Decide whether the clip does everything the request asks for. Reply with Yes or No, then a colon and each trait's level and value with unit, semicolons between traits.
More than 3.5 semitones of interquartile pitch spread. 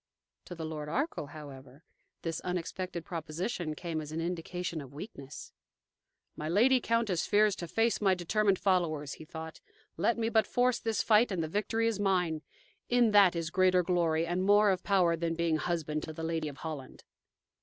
Yes: average, 4.3 semitones